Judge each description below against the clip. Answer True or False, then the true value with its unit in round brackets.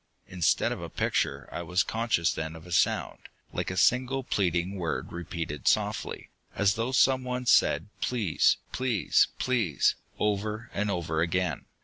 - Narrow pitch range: False (5.6 semitones)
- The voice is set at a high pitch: False (95 Hz)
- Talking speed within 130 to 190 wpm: True (145 wpm)